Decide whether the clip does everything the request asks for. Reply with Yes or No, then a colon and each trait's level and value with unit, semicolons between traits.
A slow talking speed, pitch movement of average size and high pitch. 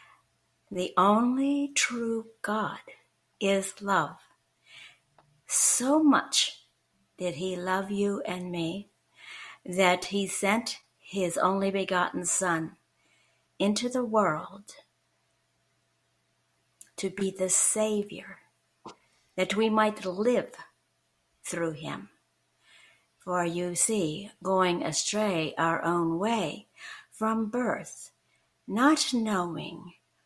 Yes: slow, 90 wpm; average, 3.6 semitones; high, 195 Hz